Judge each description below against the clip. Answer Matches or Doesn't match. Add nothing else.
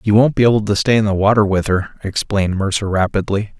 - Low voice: Matches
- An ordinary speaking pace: Doesn't match